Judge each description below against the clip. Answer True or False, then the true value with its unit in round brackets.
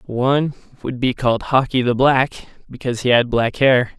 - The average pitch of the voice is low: True (125 Hz)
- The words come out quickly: False (180 wpm)